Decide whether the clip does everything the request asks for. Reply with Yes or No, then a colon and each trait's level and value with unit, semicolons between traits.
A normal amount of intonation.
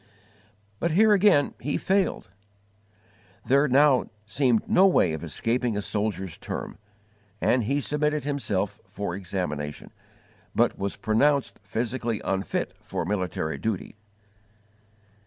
No: wide, 6.7 semitones